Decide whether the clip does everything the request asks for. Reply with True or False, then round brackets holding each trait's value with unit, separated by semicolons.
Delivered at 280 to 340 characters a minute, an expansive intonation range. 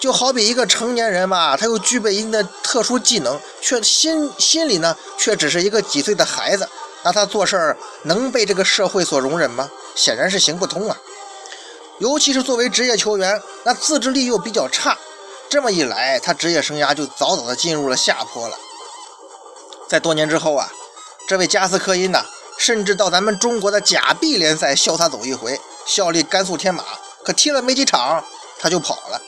True (285 characters per minute; 6.6 semitones)